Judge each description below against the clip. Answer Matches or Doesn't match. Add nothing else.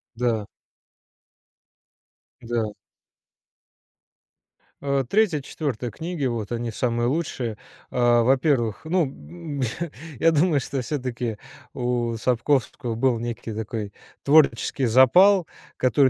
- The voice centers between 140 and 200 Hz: Doesn't match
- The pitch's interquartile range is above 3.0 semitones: Matches